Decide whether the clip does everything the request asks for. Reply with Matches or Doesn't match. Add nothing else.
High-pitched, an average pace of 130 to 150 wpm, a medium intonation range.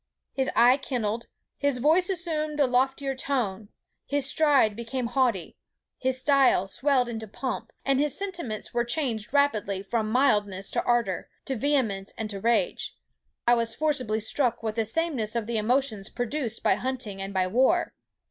Doesn't match